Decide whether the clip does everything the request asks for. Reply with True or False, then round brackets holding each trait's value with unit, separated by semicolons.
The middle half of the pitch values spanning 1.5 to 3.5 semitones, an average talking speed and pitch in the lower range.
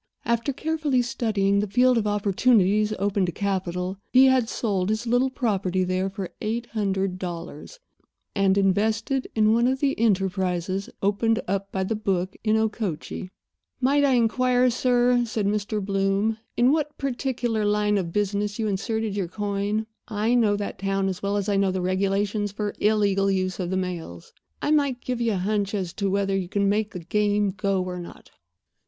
False (2.9 semitones; 180 wpm; 205 Hz)